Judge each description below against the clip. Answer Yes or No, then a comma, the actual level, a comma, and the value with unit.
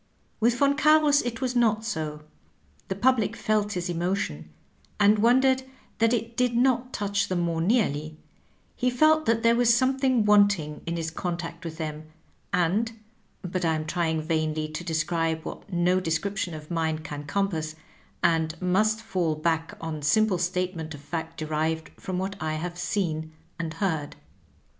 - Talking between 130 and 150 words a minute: No, average, 160 wpm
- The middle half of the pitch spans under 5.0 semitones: No, wide, 5.5 semitones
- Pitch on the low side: No, medium, 180 Hz